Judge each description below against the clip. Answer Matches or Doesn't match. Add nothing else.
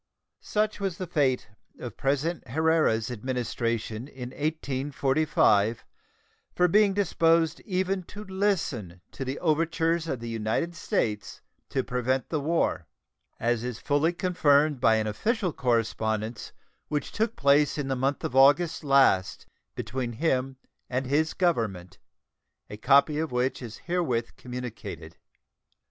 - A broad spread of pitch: Matches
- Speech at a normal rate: Doesn't match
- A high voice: Doesn't match